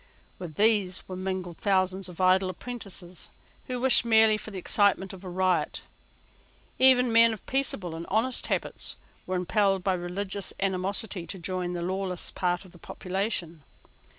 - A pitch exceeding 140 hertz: Yes, high, 190 Hz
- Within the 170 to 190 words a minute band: No, average, 155 wpm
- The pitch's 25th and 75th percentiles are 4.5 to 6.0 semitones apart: No, average, 2.7 semitones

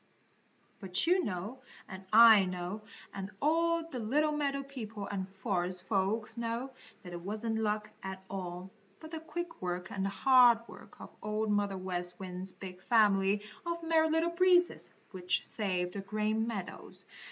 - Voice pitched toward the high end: Yes, high, 210 Hz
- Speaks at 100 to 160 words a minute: Yes, average, 155 wpm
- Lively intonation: Yes, wide, 5.7 semitones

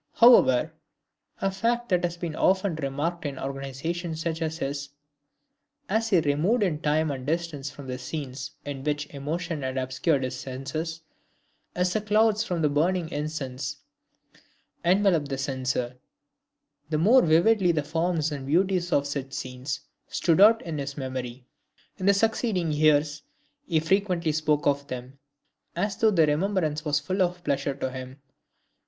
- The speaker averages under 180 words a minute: Yes, average, 155 wpm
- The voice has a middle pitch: Yes, medium, 155 Hz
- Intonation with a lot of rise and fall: No, average, 4.4 semitones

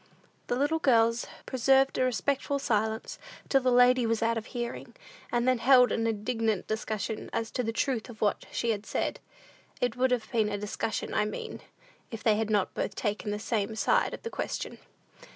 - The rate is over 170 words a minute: Yes, average, 190 wpm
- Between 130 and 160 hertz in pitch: No, high, 230 Hz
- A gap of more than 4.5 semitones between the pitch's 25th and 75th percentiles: No, narrow, 2.5 semitones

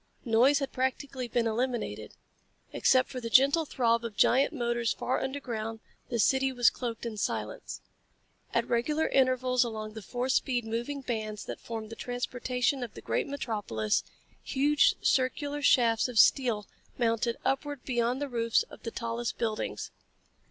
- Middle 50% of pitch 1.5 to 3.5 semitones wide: Yes, narrow, 2.5 semitones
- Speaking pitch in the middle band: No, high, 245 Hz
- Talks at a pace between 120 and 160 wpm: Yes, average, 150 wpm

